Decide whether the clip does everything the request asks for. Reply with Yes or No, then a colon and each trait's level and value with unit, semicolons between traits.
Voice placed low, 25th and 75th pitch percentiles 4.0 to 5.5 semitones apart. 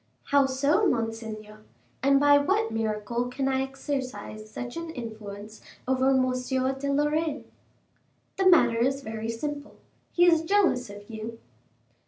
No: very high, 260 Hz; average, 4.3 semitones